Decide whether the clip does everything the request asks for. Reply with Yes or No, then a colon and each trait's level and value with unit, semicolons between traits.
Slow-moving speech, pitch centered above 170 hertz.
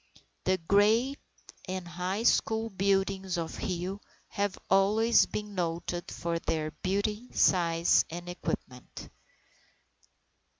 Yes: slow, 100 wpm; high, 190 Hz